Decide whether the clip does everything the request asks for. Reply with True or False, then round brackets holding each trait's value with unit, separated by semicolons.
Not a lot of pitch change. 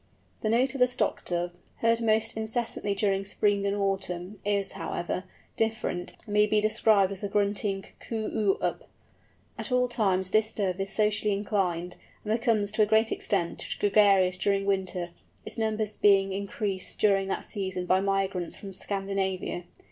True (2.0 semitones)